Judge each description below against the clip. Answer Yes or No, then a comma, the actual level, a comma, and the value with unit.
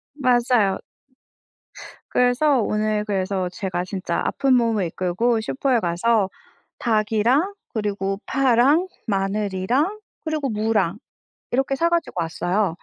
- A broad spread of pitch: No, average, 4.8 semitones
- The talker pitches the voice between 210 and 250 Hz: Yes, high, 215 Hz